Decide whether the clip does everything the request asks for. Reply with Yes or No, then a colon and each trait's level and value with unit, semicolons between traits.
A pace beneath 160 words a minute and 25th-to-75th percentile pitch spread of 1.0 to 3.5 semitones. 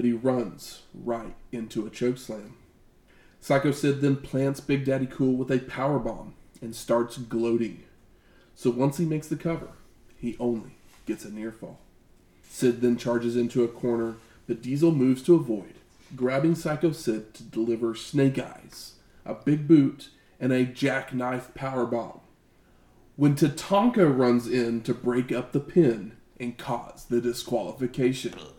Yes: average, 150 wpm; average, 2.8 semitones